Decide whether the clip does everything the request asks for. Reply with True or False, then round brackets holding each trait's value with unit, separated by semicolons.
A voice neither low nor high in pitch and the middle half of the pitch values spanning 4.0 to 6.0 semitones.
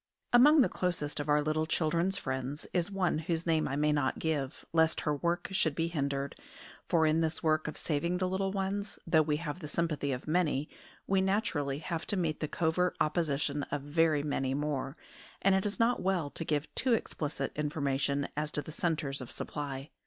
False (155 Hz; 3.2 semitones)